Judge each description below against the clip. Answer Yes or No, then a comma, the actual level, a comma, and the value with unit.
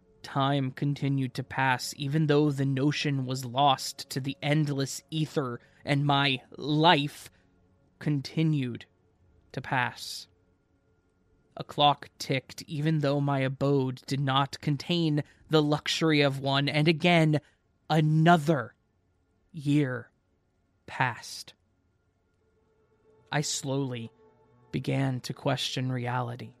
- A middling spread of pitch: Yes, average, 3.8 semitones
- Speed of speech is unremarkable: No, slow, 100 wpm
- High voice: No, low, 135 Hz